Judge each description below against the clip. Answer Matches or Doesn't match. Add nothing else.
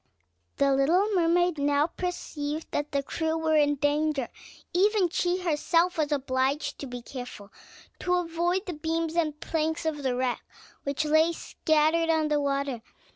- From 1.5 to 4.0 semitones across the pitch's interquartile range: Matches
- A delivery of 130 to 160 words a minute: Matches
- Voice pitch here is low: Doesn't match